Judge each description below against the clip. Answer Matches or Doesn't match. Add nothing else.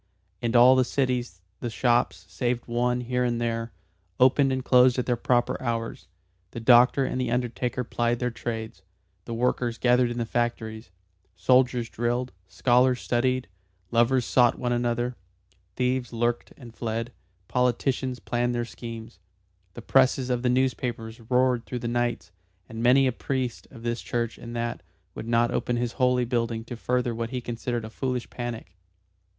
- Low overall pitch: Matches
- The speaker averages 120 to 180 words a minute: Matches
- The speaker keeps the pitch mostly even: Matches